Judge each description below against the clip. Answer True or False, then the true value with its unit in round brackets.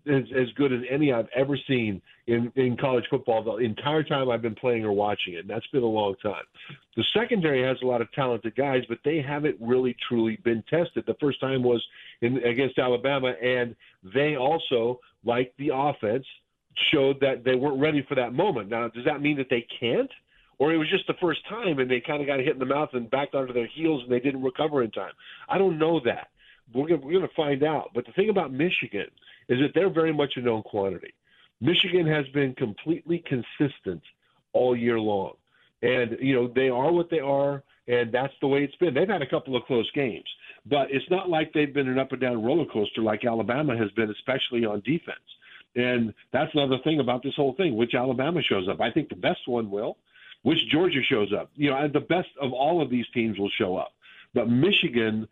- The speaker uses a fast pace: True (220 wpm)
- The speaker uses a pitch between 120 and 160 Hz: True (130 Hz)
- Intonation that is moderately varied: True (3.7 semitones)